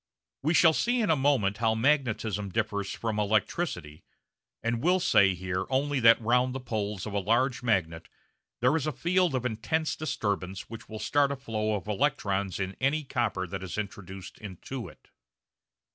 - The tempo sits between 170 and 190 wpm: Yes, average, 175 wpm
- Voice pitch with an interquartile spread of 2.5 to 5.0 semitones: No, wide, 5.4 semitones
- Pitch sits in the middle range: No, low, 115 Hz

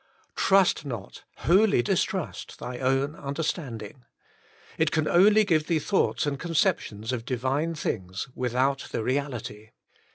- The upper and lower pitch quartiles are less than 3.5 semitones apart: No, average, 5.0 semitones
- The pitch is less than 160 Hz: Yes, medium, 140 Hz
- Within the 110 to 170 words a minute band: Yes, slow, 135 wpm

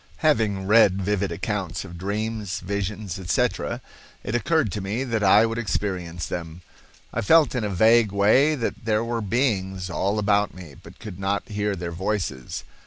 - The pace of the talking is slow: No, average, 170 wpm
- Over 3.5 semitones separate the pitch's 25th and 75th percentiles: No, average, 3.0 semitones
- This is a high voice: No, low, 100 Hz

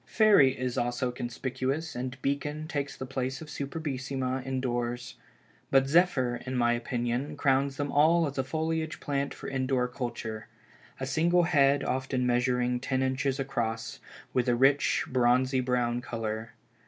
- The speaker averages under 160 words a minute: Yes, average, 145 wpm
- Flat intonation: Yes, narrow, 2.3 semitones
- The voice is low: Yes, low, 130 Hz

